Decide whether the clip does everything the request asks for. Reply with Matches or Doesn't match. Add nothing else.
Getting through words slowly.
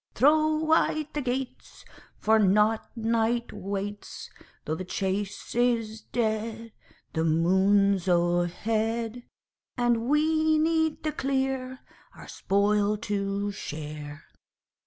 Matches